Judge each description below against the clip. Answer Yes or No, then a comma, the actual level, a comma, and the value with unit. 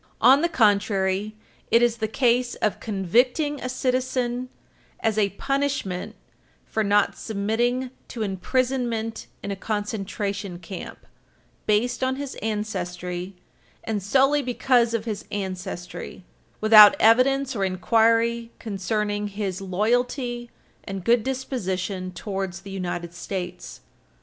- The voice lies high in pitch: Yes, high, 215 Hz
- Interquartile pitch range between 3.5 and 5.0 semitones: Yes, average, 4.1 semitones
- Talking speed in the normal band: No, slow, 115 wpm